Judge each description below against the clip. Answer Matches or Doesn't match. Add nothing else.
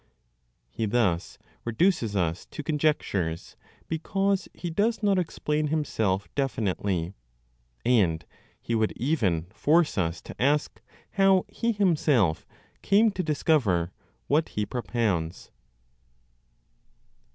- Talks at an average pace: Doesn't match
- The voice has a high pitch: Doesn't match